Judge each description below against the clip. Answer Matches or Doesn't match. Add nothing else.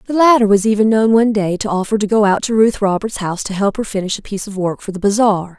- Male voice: Doesn't match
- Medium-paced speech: Doesn't match